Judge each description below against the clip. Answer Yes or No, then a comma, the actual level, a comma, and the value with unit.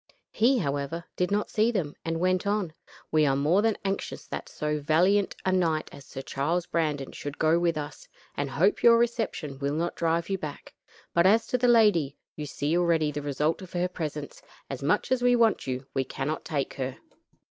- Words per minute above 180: Yes, average, 200 wpm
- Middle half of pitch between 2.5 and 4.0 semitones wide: No, average, 5.0 semitones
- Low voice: No, medium, 165 Hz